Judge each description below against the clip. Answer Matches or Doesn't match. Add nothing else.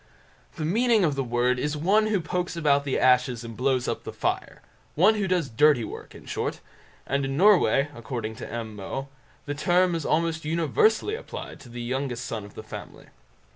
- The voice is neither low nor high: Matches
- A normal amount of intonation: Doesn't match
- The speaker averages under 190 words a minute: Doesn't match